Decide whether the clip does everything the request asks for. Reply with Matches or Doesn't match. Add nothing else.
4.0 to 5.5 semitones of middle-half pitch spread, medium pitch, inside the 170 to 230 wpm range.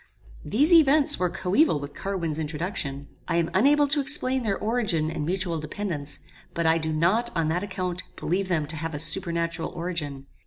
Matches